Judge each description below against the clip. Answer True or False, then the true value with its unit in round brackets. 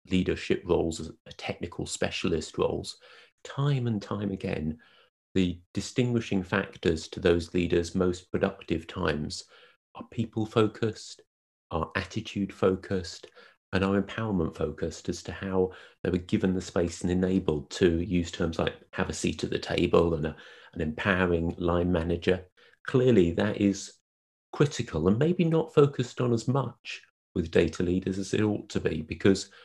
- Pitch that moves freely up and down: False (3.6 semitones)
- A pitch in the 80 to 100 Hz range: True (95 Hz)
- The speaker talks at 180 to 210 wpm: False (155 wpm)